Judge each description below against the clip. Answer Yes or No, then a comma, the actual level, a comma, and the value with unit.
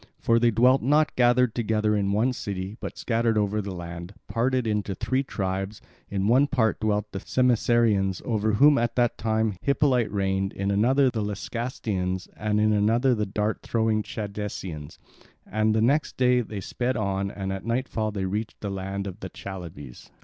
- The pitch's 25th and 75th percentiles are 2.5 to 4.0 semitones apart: Yes, average, 3.3 semitones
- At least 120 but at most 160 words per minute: No, average, 175 wpm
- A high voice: No, low, 105 Hz